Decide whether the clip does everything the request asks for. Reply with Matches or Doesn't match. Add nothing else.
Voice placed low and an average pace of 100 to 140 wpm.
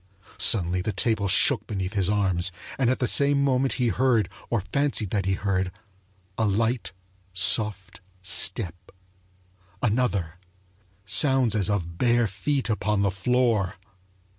Matches